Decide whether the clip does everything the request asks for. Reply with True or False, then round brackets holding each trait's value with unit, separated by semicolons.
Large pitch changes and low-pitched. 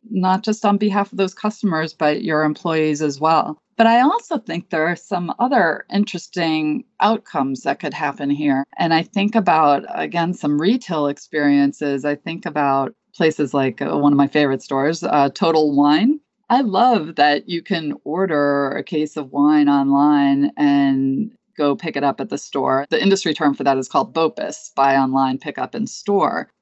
False (6.1 semitones; 160 Hz)